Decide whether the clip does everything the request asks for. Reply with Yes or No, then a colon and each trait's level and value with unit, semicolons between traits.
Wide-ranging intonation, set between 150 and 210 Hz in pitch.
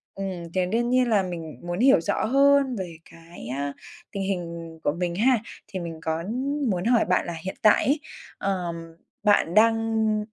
No: average, 4.8 semitones; high, 190 Hz